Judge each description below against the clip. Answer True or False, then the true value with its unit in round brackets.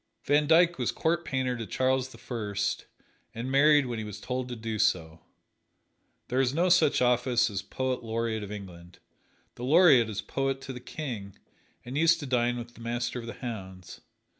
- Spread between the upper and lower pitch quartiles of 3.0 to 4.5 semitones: True (3.6 semitones)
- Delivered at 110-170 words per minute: False (190 wpm)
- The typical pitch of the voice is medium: False (125 Hz)